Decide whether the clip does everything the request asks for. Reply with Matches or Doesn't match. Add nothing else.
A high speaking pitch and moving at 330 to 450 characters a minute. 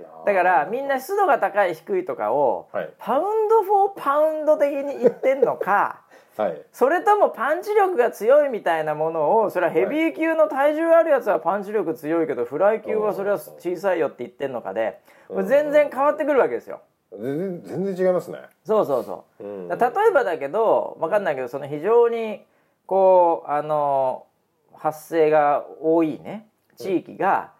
Matches